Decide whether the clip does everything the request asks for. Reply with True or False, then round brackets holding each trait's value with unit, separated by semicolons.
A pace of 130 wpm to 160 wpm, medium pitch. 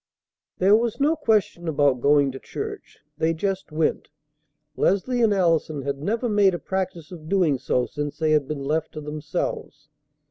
False (170 wpm; 160 Hz)